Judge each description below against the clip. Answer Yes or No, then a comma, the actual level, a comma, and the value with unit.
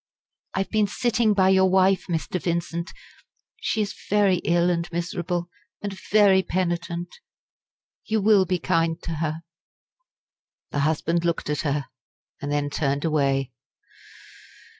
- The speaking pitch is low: No, medium, 175 Hz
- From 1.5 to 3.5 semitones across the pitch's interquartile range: Yes, average, 2.9 semitones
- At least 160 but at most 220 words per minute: No, slow, 135 wpm